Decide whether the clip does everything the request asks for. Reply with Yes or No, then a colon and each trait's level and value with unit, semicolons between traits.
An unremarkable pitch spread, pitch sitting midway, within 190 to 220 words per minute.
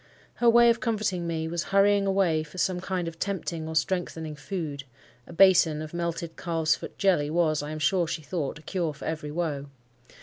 Yes: average, 3.3 semitones; medium, 165 Hz; average, 195 wpm